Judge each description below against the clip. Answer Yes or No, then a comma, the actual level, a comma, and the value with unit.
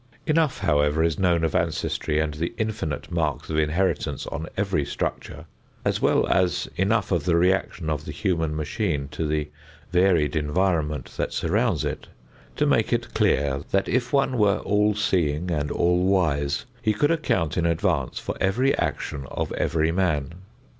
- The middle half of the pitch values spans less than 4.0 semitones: No, average, 4.3 semitones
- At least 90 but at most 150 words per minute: No, average, 165 wpm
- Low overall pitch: Yes, very low, 85 Hz